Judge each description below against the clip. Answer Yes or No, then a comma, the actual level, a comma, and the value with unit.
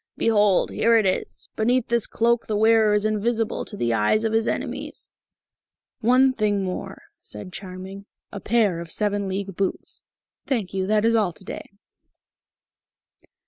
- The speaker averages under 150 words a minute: No, average, 155 wpm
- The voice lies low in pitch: No, high, 210 Hz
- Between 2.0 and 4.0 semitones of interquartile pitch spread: Yes, average, 2.8 semitones